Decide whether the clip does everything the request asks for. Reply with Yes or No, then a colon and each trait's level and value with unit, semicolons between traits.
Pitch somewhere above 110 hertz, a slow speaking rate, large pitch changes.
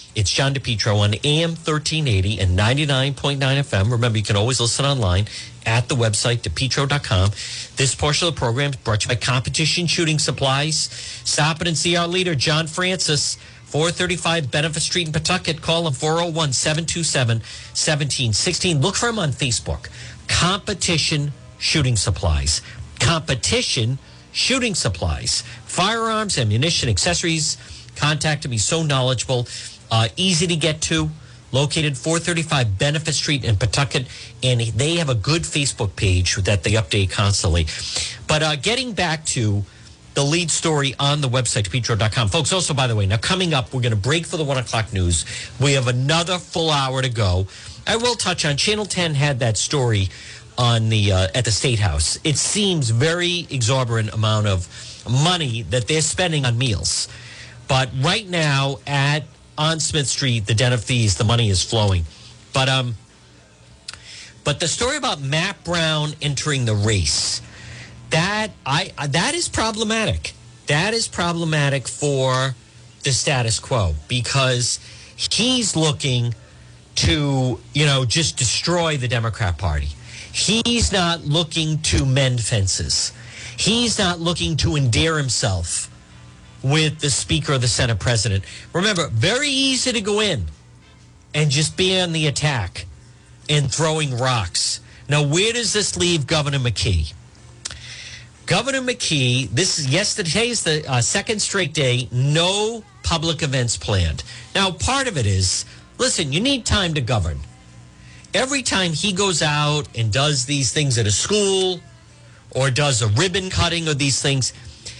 No: low, 135 Hz; average, 150 wpm; wide, 6.2 semitones